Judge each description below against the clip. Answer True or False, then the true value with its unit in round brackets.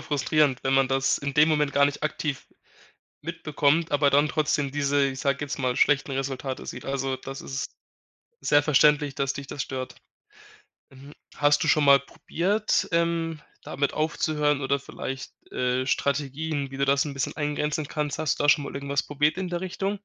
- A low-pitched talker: False (145 Hz)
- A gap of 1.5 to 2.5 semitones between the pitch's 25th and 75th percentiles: True (1.8 semitones)